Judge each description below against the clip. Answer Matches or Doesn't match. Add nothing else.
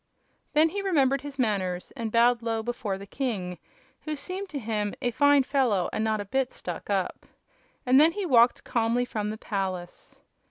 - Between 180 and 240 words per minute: Matches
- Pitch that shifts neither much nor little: Matches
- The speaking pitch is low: Doesn't match